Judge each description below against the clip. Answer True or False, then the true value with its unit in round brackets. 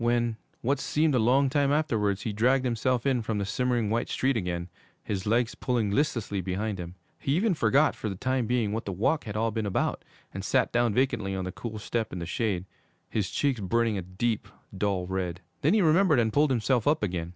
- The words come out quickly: True (220 wpm)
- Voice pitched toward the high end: False (115 Hz)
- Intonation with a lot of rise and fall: False (4.5 semitones)